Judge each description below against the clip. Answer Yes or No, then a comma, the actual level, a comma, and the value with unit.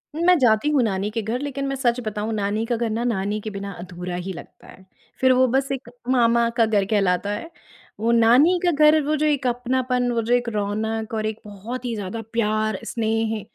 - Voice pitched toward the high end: Yes, high, 230 Hz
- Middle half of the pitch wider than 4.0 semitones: No, average, 3.3 semitones